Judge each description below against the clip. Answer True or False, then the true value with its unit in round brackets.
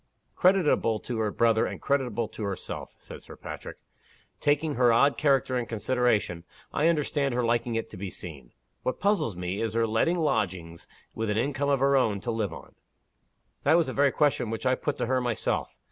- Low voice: True (120 Hz)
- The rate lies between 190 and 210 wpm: True (195 wpm)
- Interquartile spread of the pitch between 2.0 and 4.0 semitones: False (4.5 semitones)